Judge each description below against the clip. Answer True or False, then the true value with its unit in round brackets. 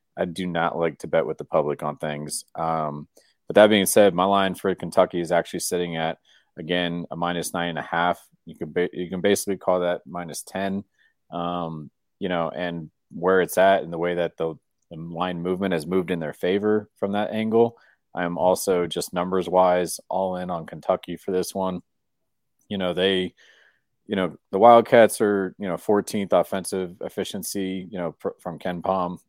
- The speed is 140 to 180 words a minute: False (195 wpm)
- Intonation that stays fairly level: True (1.9 semitones)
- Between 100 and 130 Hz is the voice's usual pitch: False (90 Hz)